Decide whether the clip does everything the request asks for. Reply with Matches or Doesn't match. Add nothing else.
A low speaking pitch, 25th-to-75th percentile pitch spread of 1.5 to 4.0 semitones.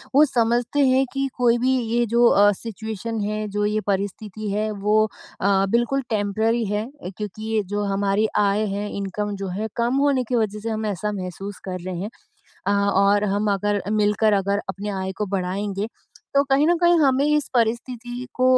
Doesn't match